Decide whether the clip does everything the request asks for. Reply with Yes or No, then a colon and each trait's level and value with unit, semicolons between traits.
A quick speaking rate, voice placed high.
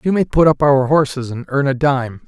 No: fast, 265 wpm; medium, 140 Hz